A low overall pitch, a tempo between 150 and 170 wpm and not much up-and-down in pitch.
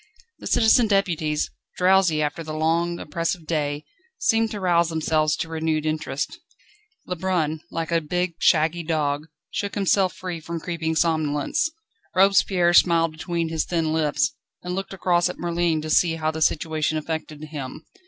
No: medium, 165 Hz; average, 155 wpm; narrow, 2.3 semitones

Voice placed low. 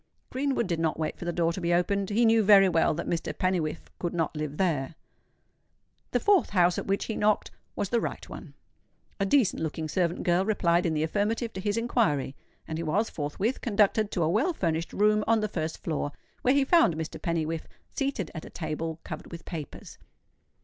No: medium, 180 Hz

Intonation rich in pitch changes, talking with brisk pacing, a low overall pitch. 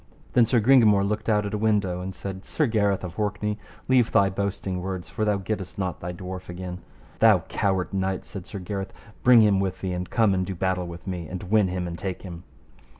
No: narrow, 2.4 semitones; fast, 220 wpm; very low, 95 Hz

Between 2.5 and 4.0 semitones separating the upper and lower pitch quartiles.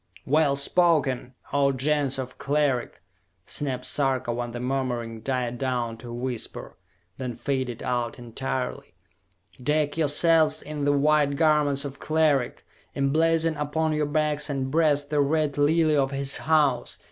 Yes: average, 2.9 semitones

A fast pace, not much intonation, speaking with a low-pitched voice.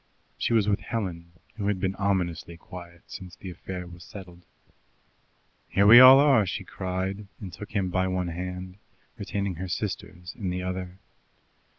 No: average, 165 wpm; narrow, 2.0 semitones; very low, 95 Hz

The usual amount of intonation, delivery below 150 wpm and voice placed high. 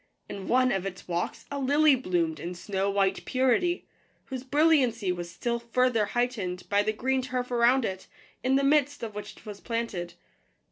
No: average, 5.0 semitones; average, 180 wpm; high, 235 Hz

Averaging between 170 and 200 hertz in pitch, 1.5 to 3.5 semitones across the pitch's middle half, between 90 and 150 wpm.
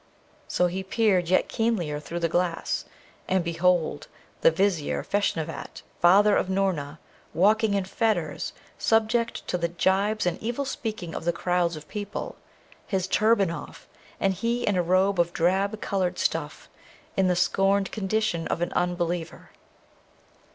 Yes: medium, 185 Hz; average, 3.0 semitones; average, 145 wpm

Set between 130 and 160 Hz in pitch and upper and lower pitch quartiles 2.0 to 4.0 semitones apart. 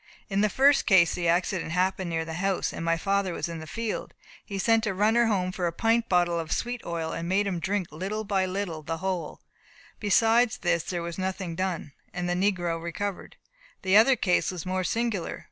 No: medium, 185 Hz; average, 3.2 semitones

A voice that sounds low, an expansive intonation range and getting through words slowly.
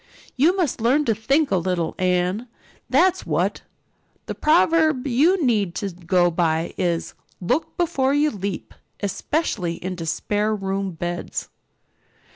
No: high, 205 Hz; wide, 8.4 semitones; slow, 130 wpm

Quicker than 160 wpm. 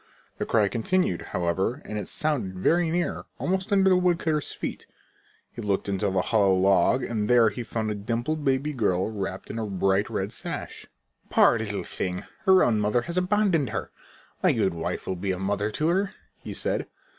Yes: average, 190 wpm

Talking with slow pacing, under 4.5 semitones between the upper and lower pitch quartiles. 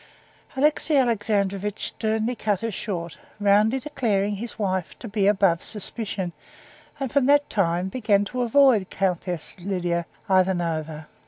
Yes: slow, 130 wpm; average, 3.7 semitones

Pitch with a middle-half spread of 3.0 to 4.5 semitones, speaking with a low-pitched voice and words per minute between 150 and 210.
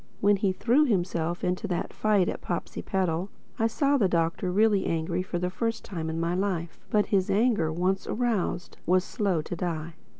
No: average, 3.4 semitones; medium, 185 Hz; average, 180 wpm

